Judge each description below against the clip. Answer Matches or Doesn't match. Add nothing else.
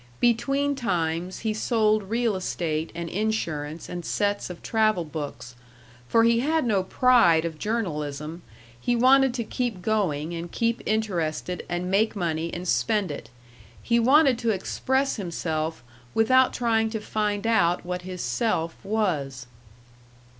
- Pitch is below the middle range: Doesn't match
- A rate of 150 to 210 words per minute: Doesn't match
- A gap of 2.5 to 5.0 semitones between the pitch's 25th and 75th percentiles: Doesn't match